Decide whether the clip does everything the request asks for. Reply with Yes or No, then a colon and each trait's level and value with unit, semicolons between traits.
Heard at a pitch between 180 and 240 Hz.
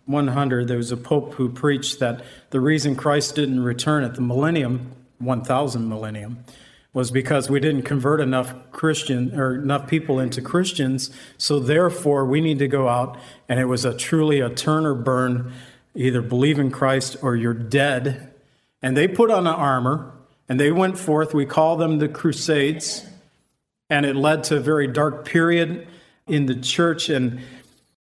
No: medium, 140 Hz